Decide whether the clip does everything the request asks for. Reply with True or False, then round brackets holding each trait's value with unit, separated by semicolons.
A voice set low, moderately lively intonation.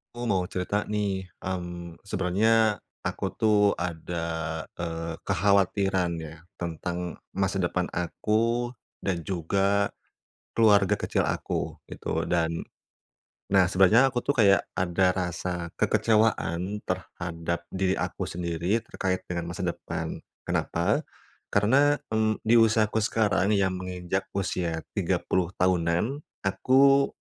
True (95 Hz; 3.3 semitones)